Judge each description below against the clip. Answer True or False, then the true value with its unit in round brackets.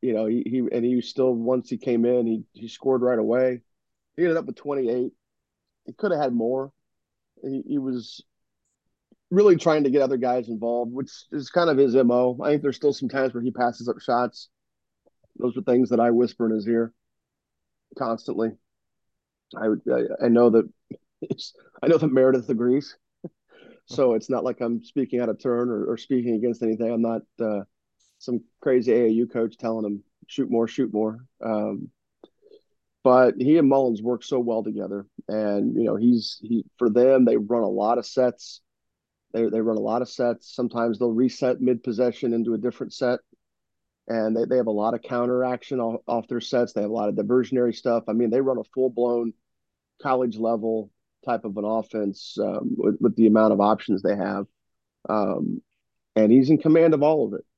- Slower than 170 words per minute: False (195 wpm)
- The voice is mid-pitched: False (120 Hz)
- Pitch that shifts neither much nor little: False (2.3 semitones)